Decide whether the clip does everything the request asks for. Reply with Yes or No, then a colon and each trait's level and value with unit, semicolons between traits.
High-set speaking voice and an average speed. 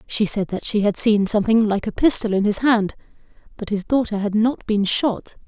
No: high, 215 Hz; fast, 220 wpm